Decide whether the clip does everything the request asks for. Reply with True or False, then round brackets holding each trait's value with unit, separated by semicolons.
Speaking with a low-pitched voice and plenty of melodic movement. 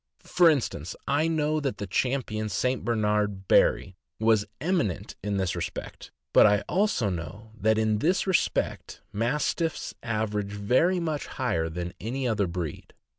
True (110 Hz; 5.9 semitones)